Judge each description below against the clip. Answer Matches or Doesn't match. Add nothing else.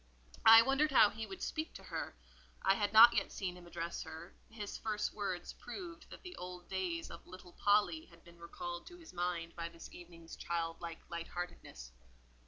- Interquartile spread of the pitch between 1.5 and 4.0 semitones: Doesn't match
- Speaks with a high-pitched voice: Doesn't match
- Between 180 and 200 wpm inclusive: Matches